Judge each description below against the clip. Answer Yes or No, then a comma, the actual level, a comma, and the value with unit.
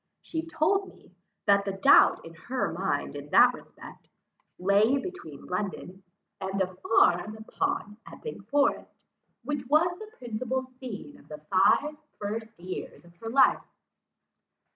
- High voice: Yes, high, 225 Hz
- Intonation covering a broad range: Yes, wide, 7.1 semitones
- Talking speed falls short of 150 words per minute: Yes, average, 140 wpm